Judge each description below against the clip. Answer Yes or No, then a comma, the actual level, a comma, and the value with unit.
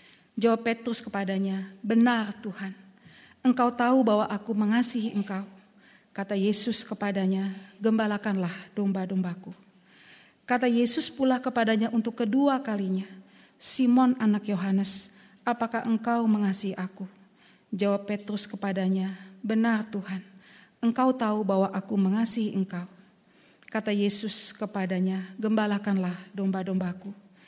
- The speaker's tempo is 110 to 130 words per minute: No, average, 100 wpm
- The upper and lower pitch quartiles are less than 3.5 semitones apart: Yes, narrow, 2.6 semitones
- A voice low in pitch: No, high, 205 Hz